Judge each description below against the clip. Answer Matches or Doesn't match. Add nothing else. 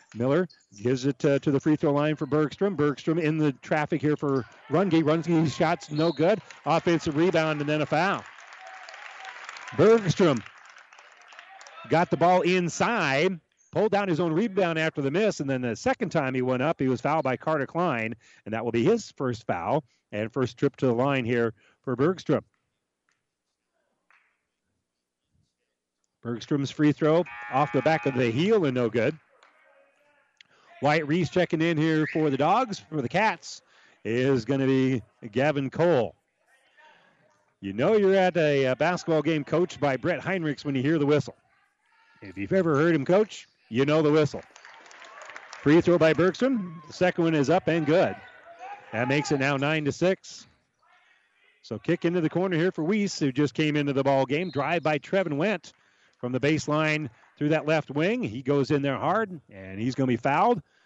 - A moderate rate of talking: Matches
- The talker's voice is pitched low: Doesn't match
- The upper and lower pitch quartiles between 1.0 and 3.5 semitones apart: Doesn't match